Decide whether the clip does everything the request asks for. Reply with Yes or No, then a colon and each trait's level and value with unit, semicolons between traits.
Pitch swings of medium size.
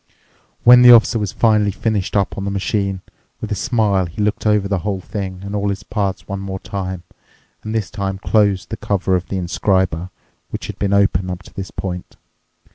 No: narrow, 1.9 semitones